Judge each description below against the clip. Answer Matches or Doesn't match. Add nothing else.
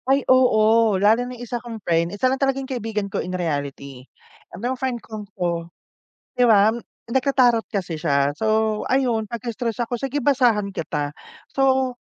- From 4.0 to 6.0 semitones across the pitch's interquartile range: Matches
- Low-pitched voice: Doesn't match